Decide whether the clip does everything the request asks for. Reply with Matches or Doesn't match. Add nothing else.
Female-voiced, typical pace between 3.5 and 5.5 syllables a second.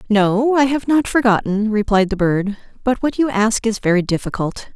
Matches